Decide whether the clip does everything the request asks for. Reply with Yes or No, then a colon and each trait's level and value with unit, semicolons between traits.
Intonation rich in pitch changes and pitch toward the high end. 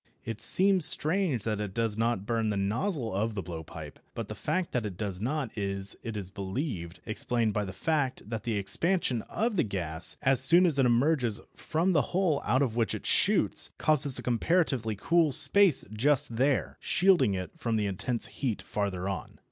No: wide, 6.7 semitones; low, 115 Hz